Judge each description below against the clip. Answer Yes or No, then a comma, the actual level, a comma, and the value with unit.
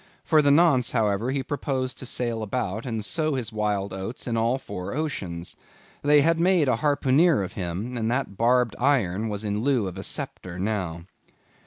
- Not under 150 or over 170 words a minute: No, average, 185 wpm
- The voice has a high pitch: No, low, 115 Hz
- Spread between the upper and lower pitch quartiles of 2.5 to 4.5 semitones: No, average, 5.3 semitones